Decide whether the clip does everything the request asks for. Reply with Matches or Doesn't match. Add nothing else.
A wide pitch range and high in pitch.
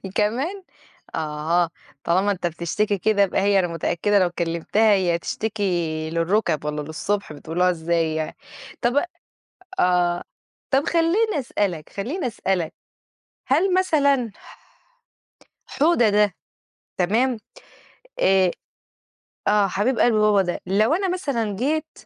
Matches